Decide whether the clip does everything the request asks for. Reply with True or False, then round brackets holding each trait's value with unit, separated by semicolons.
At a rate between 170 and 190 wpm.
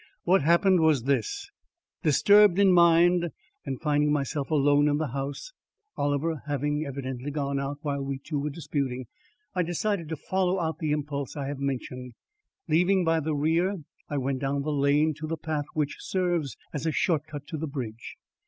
True (180 wpm)